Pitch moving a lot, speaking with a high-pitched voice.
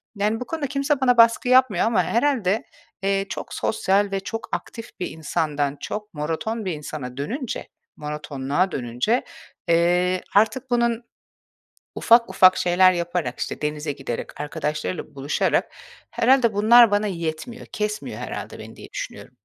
Yes: wide, 6.8 semitones; high, 195 Hz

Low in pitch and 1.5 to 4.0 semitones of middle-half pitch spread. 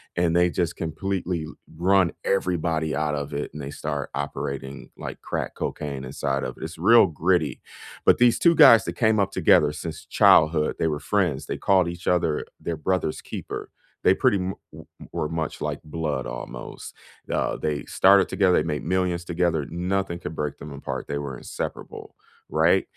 Yes: very low, 80 Hz; average, 3.7 semitones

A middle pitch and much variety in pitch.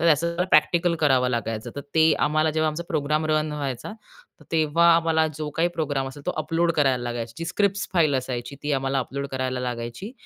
No: medium, 150 Hz; average, 3.8 semitones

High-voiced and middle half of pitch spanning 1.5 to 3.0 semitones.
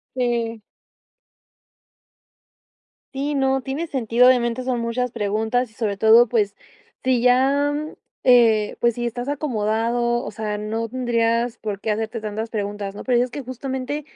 Yes: high, 240 Hz; narrow, 2.6 semitones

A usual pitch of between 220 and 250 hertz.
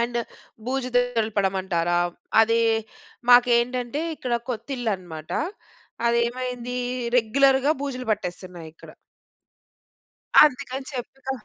Yes: high, 245 Hz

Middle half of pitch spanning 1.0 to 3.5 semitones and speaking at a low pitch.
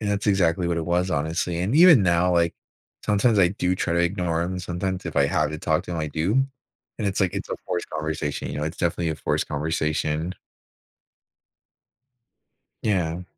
Yes: average, 2.8 semitones; very low, 85 Hz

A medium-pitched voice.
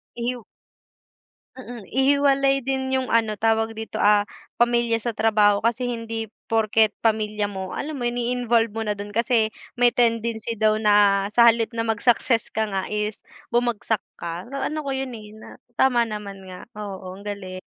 No: high, 225 Hz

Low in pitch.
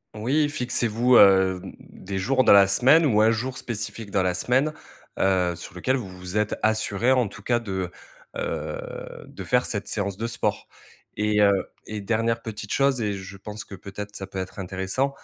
Yes: low, 105 Hz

